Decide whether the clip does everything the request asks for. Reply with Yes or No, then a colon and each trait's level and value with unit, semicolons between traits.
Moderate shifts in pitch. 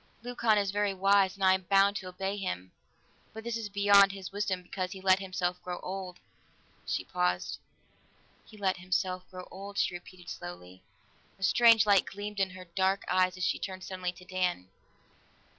No: narrow, 1.6 semitones